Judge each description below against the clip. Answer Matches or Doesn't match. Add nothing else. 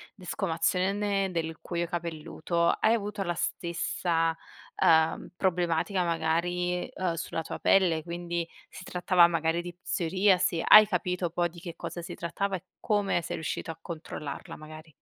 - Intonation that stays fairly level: Matches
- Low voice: Doesn't match